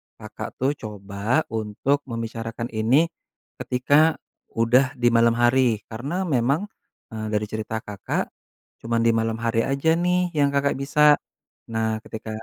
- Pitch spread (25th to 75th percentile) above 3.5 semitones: Yes, average, 4.0 semitones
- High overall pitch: No, low, 115 Hz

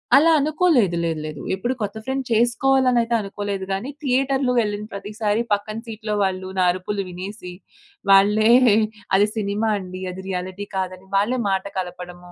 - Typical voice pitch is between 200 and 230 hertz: Yes, high, 205 Hz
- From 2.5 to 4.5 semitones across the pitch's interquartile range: Yes, average, 3.9 semitones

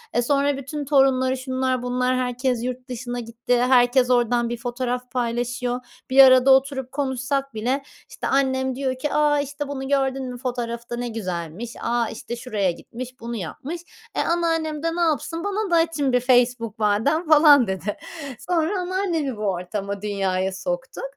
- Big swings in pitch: No, average, 3.0 semitones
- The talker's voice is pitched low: No, very high, 255 Hz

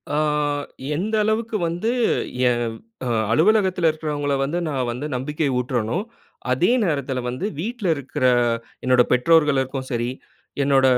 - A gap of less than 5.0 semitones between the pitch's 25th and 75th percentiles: No, average, 5.3 semitones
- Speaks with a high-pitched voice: No, medium, 145 Hz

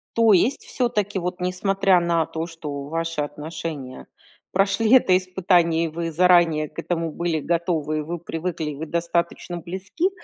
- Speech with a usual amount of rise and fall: No, narrow, 2.3 semitones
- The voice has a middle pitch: Yes, medium, 170 Hz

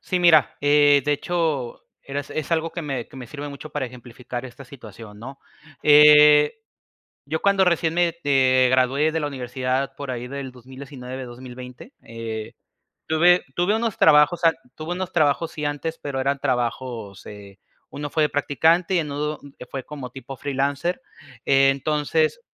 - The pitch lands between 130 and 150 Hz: Yes, medium, 140 Hz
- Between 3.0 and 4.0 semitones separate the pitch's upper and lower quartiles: Yes, average, 3.5 semitones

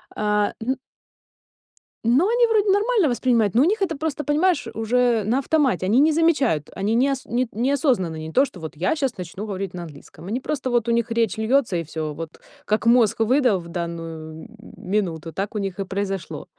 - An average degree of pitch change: No, wide, 6.7 semitones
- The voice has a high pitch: Yes, high, 225 Hz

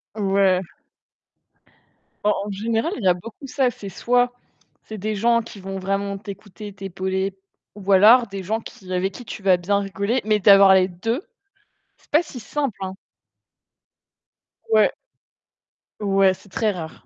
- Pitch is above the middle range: Yes, high, 200 Hz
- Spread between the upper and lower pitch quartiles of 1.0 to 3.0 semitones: Yes, narrow, 2.6 semitones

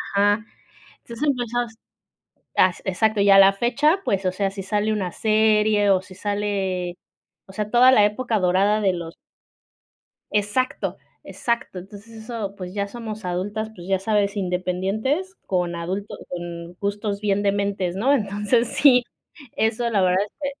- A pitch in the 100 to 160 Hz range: No, high, 205 Hz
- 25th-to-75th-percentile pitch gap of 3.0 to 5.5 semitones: No, narrow, 2.6 semitones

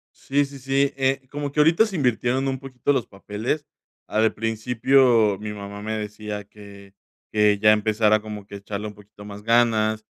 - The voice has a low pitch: Yes, low, 110 Hz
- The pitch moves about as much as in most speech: Yes, average, 4.3 semitones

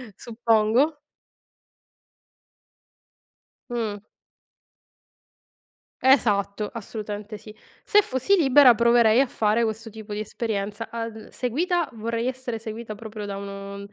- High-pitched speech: Yes, high, 225 Hz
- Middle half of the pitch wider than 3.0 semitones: No, narrow, 2.5 semitones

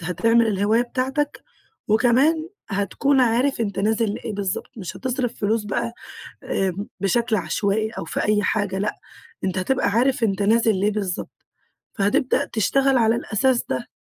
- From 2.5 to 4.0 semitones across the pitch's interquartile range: Yes, average, 3.4 semitones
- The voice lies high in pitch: Yes, high, 220 Hz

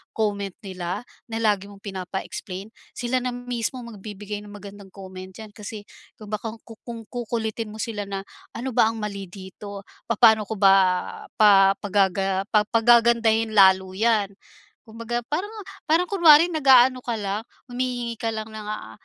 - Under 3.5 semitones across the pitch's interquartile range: Yes, average, 2.9 semitones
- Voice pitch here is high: Yes, high, 215 Hz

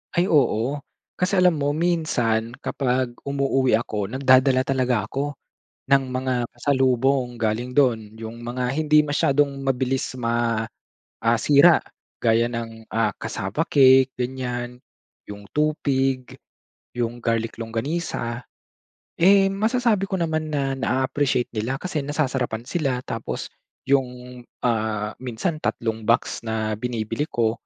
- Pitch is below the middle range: Yes, low, 130 Hz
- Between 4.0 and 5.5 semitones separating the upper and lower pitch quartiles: No, average, 3.5 semitones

